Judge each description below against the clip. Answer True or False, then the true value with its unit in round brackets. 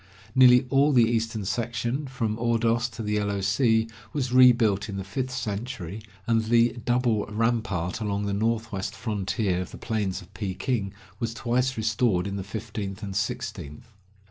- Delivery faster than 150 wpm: True (160 wpm)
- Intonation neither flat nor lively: True (3.2 semitones)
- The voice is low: True (110 Hz)